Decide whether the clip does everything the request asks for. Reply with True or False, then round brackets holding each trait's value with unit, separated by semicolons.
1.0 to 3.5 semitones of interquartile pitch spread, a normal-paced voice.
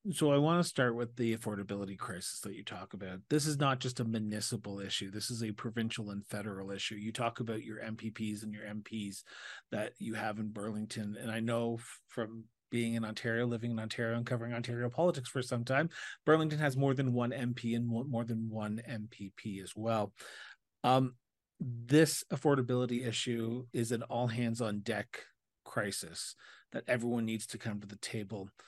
True (2.4 semitones; 185 wpm)